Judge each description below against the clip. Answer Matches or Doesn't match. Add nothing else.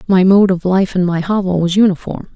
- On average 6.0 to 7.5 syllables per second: Doesn't match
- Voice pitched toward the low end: Doesn't match